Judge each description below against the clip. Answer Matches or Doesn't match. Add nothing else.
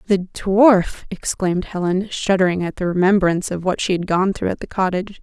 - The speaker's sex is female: Matches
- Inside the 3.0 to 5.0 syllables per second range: Doesn't match